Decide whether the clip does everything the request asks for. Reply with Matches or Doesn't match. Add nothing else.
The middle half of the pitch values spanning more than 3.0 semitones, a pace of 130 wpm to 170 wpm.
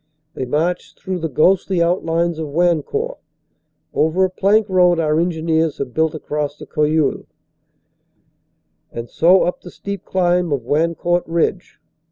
Doesn't match